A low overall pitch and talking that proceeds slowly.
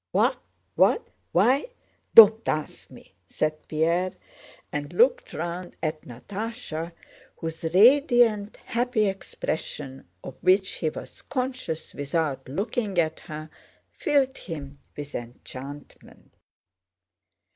No: medium, 170 Hz; slow, 95 wpm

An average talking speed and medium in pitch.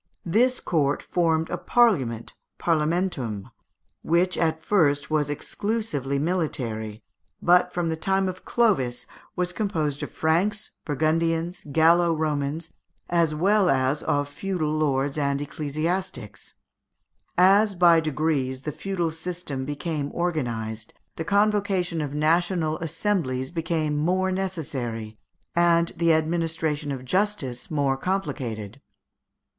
No: slow, 115 wpm; medium, 160 Hz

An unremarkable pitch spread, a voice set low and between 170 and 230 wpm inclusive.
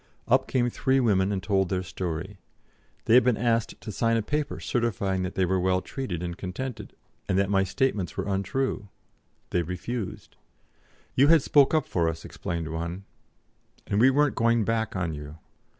Yes: average, 5.0 semitones; low, 100 Hz; average, 180 wpm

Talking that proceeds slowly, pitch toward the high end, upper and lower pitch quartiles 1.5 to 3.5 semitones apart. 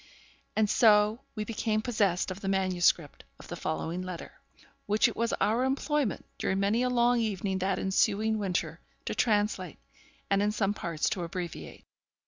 No: average, 160 wpm; high, 205 Hz; average, 2.9 semitones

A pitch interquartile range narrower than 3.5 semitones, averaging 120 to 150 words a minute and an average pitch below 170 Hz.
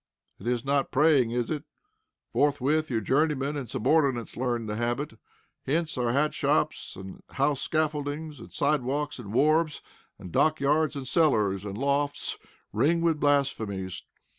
No: average, 4.0 semitones; average, 145 wpm; medium, 140 Hz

